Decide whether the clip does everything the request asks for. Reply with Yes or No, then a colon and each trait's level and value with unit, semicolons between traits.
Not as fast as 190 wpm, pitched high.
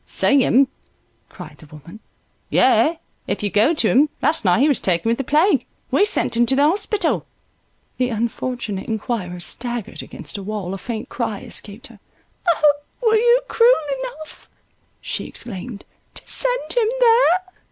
Yes: average, 165 wpm; high, 245 Hz